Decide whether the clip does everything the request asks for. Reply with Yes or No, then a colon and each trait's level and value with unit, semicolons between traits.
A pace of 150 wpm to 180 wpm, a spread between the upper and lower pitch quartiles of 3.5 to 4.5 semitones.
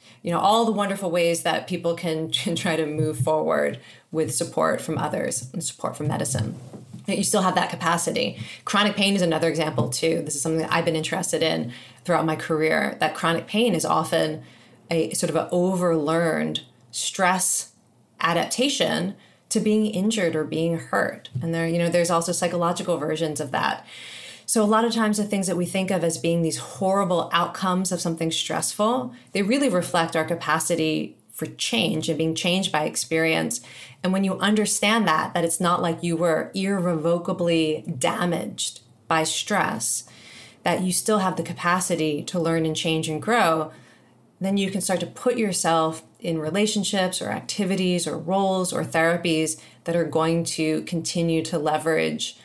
No: average, 175 wpm; average, 2.7 semitones